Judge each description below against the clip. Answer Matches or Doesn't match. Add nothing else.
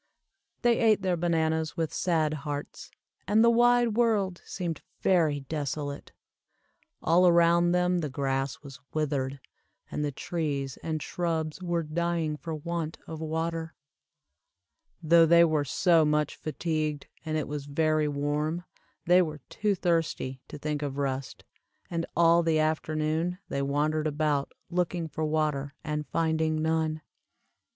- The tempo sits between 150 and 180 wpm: Doesn't match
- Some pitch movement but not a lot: Doesn't match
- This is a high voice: Doesn't match